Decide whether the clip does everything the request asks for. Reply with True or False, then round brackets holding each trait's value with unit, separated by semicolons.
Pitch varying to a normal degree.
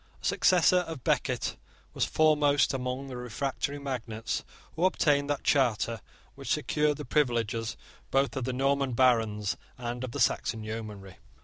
True (3.7 semitones)